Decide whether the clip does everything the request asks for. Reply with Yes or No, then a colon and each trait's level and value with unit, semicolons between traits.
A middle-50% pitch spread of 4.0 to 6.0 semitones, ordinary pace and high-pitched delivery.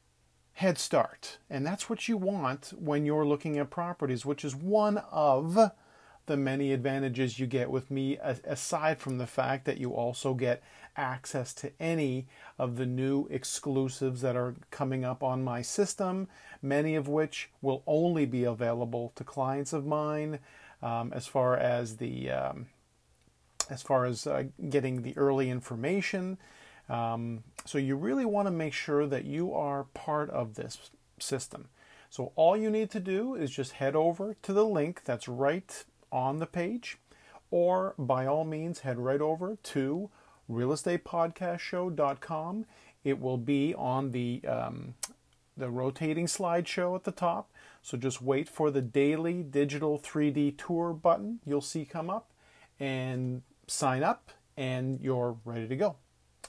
No: average, 4.4 semitones; average, 155 wpm; medium, 140 Hz